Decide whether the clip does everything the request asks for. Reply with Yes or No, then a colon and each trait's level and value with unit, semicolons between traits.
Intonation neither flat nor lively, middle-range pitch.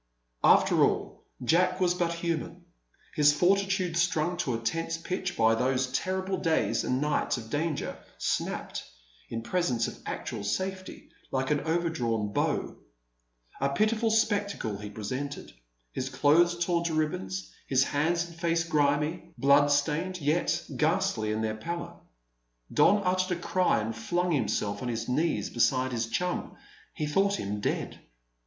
No: wide, 5.7 semitones; medium, 160 Hz